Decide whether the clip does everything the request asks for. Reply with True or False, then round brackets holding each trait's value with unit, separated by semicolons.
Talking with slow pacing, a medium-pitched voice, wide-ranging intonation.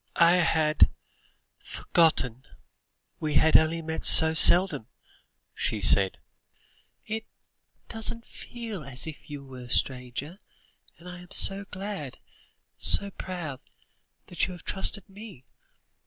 True (120 wpm; 165 Hz; 5.7 semitones)